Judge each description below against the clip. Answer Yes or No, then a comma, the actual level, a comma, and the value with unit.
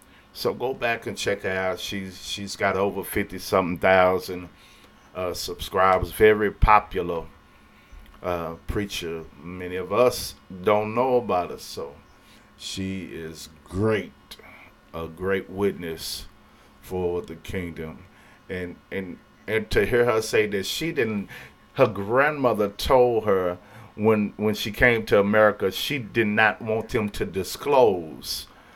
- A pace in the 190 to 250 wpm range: No, slow, 135 wpm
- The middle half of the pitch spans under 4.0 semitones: Yes, average, 3.5 semitones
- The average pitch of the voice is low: Yes, low, 100 Hz